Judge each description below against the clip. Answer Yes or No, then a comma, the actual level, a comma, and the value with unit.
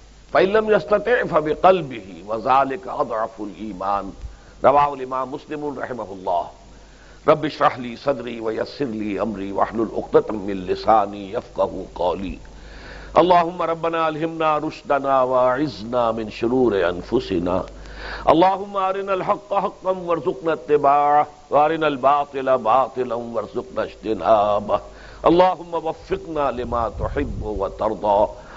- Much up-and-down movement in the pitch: Yes, wide, 6.2 semitones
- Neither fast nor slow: No, slow, 100 wpm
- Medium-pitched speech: Yes, medium, 145 Hz